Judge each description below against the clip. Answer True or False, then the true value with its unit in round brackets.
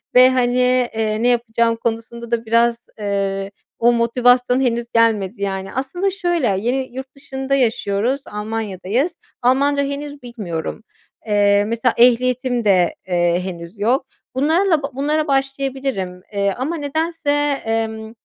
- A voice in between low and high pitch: False (240 Hz)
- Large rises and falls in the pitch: False (4.1 semitones)